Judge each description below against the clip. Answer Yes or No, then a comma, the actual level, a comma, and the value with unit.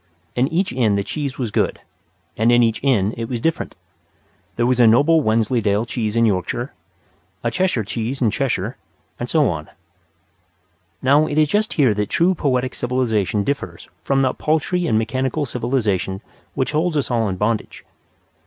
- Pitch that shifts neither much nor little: Yes, average, 4.4 semitones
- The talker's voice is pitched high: No, low, 125 Hz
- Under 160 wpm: No, average, 170 wpm